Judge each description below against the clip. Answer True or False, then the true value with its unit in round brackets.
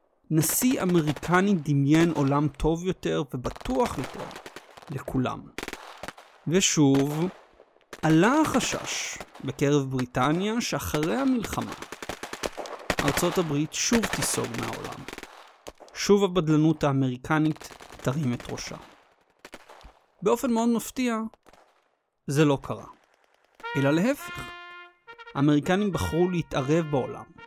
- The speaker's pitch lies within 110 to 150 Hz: False (160 Hz)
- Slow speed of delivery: True (85 wpm)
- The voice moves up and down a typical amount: False (7.3 semitones)